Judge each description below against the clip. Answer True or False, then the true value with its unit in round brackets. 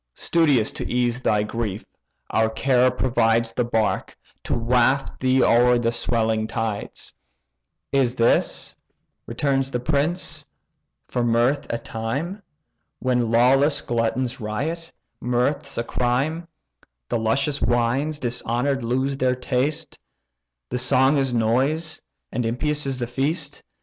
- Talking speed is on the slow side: True (125 wpm)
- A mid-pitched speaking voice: False (125 Hz)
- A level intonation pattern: False (3.0 semitones)